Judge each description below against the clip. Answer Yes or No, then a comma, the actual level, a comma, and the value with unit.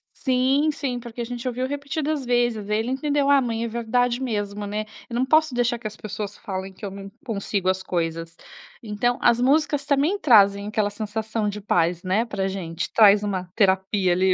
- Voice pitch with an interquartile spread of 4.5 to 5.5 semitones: No, average, 4.1 semitones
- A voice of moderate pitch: No, high, 220 Hz